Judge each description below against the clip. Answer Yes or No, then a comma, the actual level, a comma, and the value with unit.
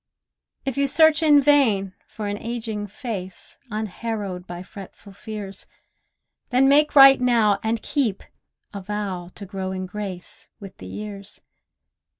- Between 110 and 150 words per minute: Yes, average, 140 wpm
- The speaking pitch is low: No, high, 210 Hz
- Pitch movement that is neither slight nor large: Yes, average, 4.3 semitones